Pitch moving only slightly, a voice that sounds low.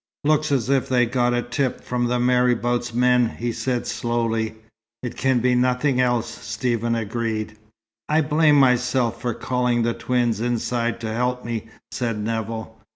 Yes: narrow, 1.5 semitones; low, 120 Hz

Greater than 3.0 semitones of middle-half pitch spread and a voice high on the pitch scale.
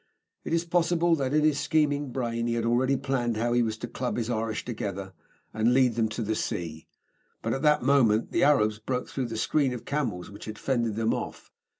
No: average, 4.1 semitones; low, 120 Hz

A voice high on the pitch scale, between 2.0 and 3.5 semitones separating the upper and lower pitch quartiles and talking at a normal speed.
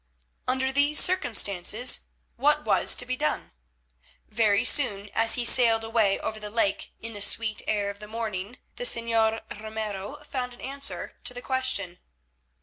Yes: high, 225 Hz; average, 3.1 semitones; average, 155 wpm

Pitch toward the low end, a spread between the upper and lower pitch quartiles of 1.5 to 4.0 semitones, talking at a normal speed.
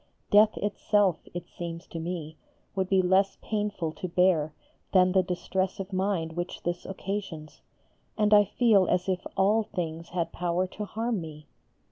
No: medium, 185 Hz; average, 2.9 semitones; average, 160 wpm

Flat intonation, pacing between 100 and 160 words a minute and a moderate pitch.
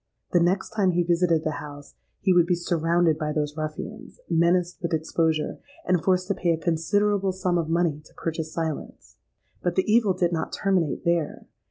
No: narrow, 2.3 semitones; average, 185 wpm; medium, 170 Hz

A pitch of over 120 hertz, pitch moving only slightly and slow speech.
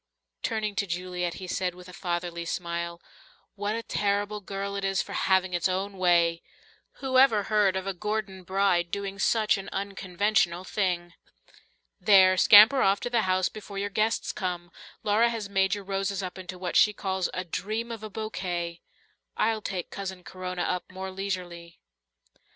No: high, 190 Hz; narrow, 2.3 semitones; average, 170 wpm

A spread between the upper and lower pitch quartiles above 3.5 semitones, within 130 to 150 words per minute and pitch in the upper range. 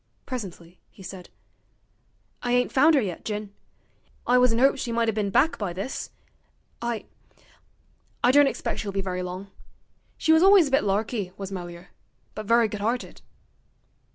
No: average, 4.4 semitones; average, 170 wpm; high, 215 Hz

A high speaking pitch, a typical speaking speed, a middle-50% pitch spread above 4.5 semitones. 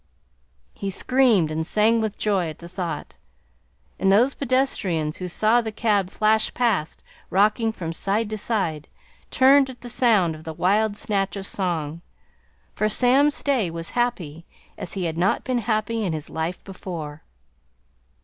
Yes: high, 200 Hz; average, 160 wpm; average, 5.2 semitones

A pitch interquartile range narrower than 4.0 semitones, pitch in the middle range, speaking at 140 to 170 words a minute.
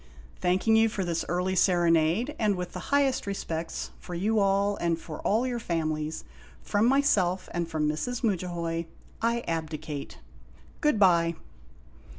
No: average, 4.8 semitones; medium, 180 Hz; average, 155 wpm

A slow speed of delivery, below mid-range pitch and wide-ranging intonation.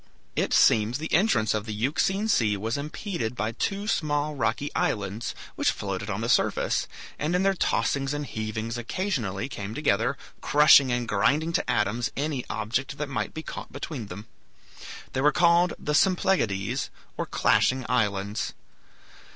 No: average, 155 wpm; low, 125 Hz; wide, 5.9 semitones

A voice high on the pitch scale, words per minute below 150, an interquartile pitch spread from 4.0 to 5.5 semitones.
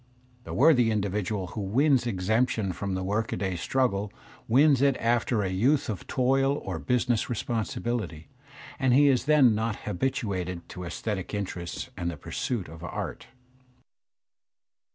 No: low, 110 Hz; average, 140 wpm; average, 5.1 semitones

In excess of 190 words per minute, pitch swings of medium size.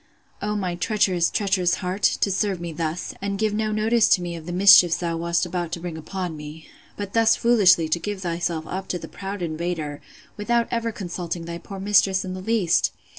Yes: average, 200 wpm; average, 3.1 semitones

